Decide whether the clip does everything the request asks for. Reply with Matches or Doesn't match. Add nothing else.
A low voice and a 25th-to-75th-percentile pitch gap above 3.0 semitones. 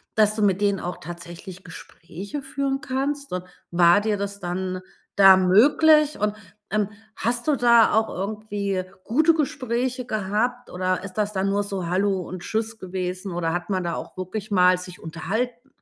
Doesn't match